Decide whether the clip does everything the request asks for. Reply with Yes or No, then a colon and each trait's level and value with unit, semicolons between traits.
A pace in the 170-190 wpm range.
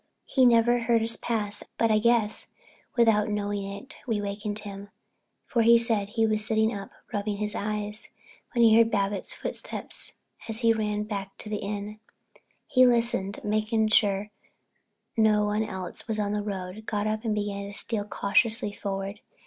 Yes: average, 175 wpm